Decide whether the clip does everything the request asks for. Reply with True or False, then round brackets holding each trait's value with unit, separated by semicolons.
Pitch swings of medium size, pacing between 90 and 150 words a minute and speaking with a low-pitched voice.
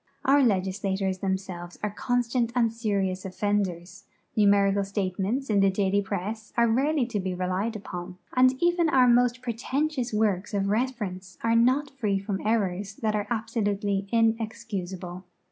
False (3.6 semitones; 145 wpm; 205 Hz)